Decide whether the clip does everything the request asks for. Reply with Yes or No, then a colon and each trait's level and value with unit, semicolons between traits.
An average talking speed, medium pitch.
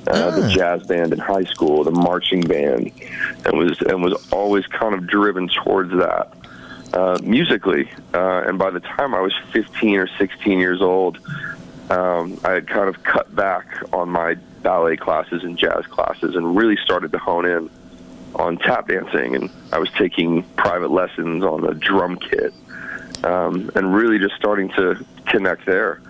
No: average, 170 wpm; very low, 90 Hz